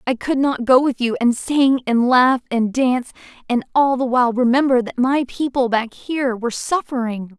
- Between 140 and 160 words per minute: No, average, 195 wpm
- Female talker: Yes, female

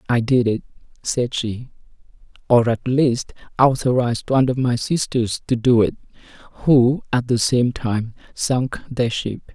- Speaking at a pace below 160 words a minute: Yes, average, 150 wpm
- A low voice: Yes, low, 120 Hz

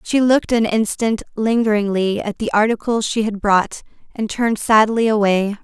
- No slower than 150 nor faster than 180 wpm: Yes, average, 160 wpm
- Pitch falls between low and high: No, high, 215 Hz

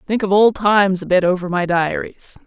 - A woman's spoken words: Yes, female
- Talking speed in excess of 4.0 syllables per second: Yes, 5.2 syllables/s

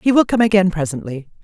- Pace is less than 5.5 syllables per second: No, 6.3 syllables/s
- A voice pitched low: No, medium, 185 Hz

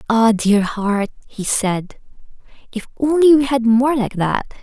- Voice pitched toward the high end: Yes, high, 235 Hz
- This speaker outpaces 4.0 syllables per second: No, 3.9 syllables/s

